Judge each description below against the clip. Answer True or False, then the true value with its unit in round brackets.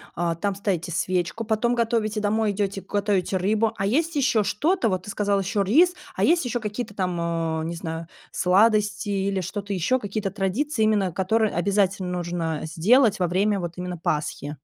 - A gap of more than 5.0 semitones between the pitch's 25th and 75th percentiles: False (3.3 semitones)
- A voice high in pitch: True (200 Hz)